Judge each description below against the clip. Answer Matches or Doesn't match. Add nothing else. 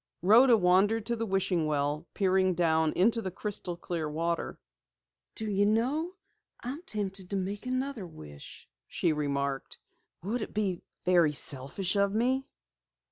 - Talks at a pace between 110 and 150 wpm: Matches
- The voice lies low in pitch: Doesn't match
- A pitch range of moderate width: Matches